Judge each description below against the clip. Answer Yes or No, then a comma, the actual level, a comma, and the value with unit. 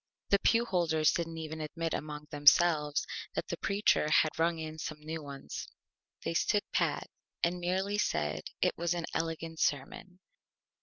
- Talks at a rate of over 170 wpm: No, average, 155 wpm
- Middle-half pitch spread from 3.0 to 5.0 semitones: No, narrow, 2.4 semitones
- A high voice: No, medium, 160 Hz